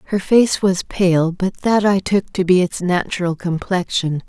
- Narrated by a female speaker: Yes, female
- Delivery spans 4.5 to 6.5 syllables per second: No, 4.2 syllables/s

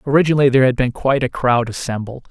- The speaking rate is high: Yes, fast, 210 wpm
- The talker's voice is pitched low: Yes, low, 130 Hz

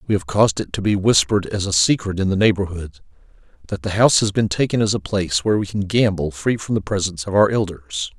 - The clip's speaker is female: No, male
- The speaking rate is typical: No, fast, 240 wpm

